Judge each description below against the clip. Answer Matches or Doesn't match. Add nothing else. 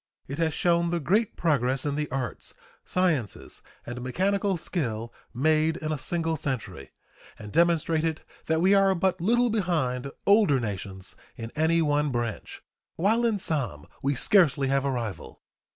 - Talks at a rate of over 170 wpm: Doesn't match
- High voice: Doesn't match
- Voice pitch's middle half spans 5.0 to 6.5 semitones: Matches